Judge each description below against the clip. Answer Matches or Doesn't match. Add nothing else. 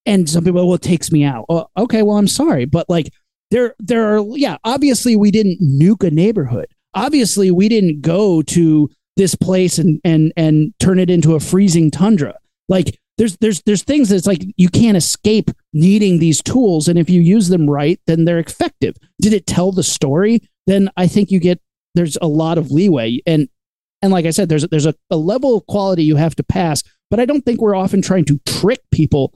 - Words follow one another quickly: Matches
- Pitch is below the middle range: Doesn't match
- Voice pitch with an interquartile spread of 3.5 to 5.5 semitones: Matches